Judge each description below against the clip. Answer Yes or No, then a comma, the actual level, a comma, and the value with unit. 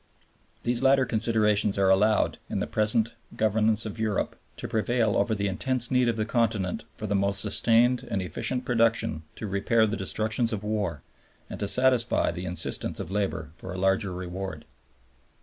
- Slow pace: No, average, 170 wpm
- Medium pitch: No, low, 110 Hz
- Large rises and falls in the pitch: No, average, 2.9 semitones